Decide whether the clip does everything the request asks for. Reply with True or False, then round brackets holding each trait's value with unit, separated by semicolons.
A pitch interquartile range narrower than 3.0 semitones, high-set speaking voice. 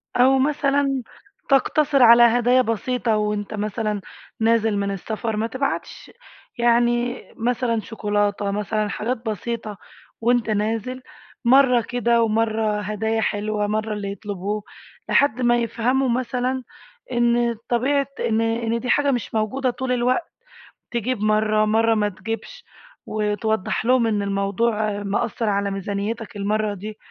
True (2.6 semitones; 225 Hz)